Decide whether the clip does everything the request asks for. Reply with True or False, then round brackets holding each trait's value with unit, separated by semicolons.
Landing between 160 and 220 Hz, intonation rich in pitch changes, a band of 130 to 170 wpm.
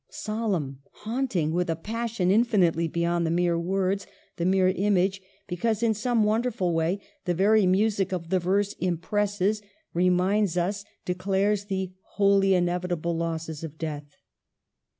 False (185 Hz; 3.1 semitones; 140 wpm)